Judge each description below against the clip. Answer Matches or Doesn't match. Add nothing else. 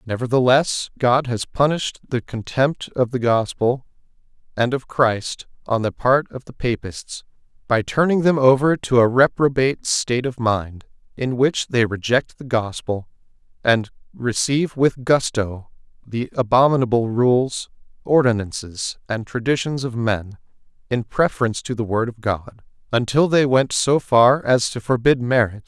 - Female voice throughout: Doesn't match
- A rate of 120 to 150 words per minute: Matches